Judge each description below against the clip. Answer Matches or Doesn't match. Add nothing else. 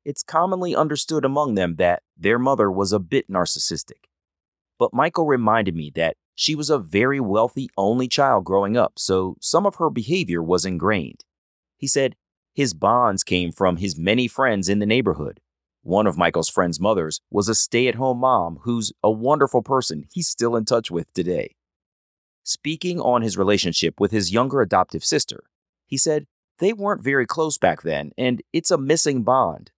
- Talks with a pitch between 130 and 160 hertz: Doesn't match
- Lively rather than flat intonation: Matches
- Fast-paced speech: Doesn't match